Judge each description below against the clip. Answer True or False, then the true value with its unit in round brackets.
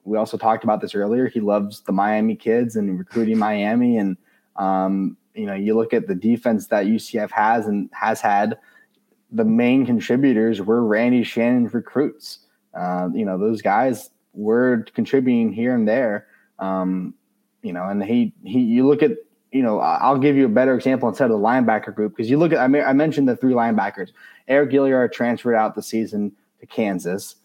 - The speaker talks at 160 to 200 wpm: True (190 wpm)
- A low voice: True (120 Hz)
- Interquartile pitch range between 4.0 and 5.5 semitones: True (4.6 semitones)